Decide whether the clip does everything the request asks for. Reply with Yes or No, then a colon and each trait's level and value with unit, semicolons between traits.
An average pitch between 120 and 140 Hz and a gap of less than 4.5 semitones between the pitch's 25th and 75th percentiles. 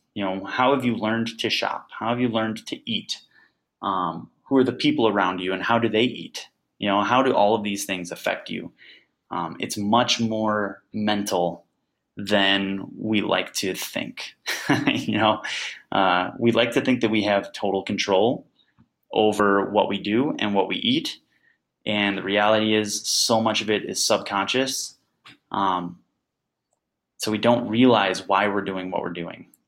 No: low, 105 Hz; average, 2.8 semitones